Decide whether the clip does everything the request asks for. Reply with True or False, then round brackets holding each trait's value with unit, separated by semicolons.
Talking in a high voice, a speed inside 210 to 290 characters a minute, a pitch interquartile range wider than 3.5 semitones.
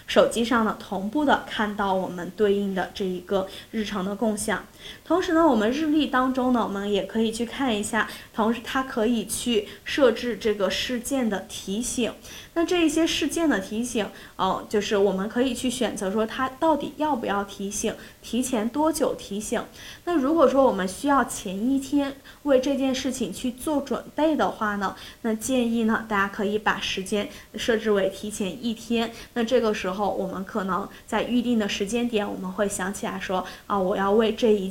True (225 Hz; 280 characters per minute; 4.1 semitones)